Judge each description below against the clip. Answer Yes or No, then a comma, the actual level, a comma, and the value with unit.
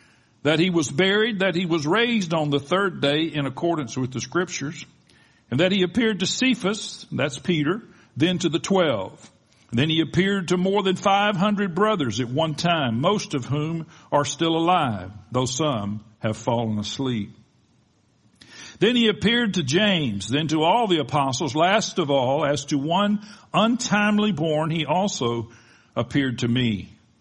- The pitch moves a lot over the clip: Yes, wide, 6.9 semitones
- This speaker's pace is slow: No, average, 165 wpm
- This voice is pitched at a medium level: Yes, medium, 160 Hz